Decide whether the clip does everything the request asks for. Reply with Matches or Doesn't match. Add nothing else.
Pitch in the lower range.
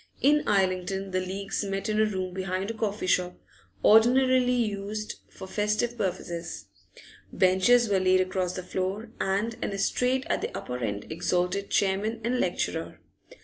Doesn't match